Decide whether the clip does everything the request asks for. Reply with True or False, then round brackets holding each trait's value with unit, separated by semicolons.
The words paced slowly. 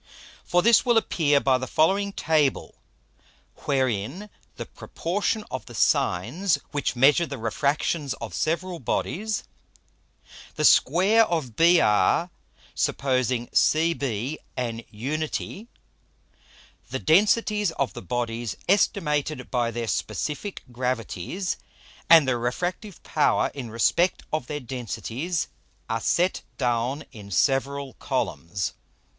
True (110 wpm)